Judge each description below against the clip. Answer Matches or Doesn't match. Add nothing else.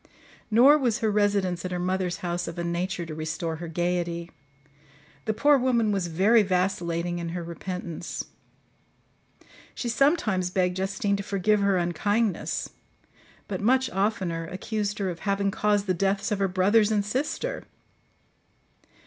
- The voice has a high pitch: Matches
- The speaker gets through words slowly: Doesn't match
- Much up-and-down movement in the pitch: Doesn't match